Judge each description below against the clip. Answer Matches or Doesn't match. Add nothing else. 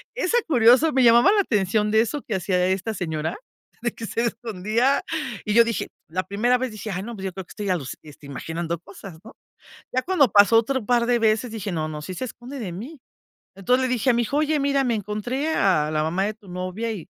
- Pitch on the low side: Doesn't match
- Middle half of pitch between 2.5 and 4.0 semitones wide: Doesn't match